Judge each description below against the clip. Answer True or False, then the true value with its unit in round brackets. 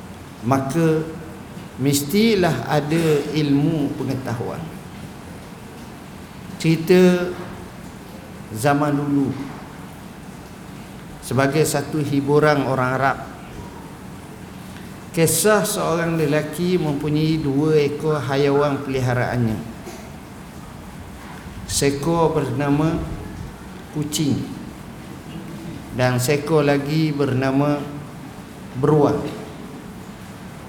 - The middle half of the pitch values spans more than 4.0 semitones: False (2.4 semitones)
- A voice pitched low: False (145 Hz)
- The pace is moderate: False (55 wpm)